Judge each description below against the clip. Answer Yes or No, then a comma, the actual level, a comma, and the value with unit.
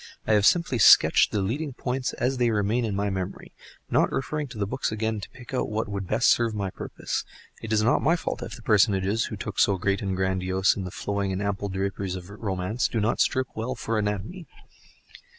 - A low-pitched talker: Yes, low, 105 Hz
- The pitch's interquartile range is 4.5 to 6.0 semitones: No, average, 3.5 semitones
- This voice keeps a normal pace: No, fast, 220 wpm